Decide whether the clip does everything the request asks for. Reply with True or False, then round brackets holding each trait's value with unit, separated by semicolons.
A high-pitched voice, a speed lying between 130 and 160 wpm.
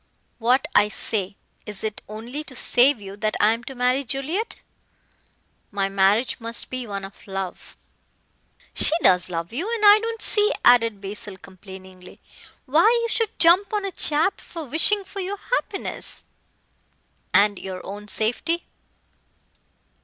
True (235 Hz; 155 wpm)